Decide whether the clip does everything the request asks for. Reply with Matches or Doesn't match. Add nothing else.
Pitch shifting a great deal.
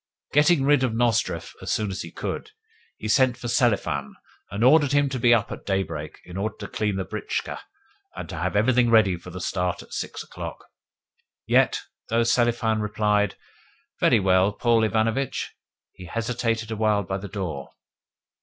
Doesn't match